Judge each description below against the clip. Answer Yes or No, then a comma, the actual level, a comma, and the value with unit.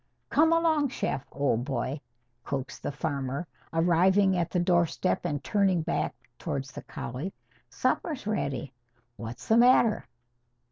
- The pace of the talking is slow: Yes, slow, 130 wpm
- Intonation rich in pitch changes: Yes, wide, 6.7 semitones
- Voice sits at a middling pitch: Yes, medium, 170 Hz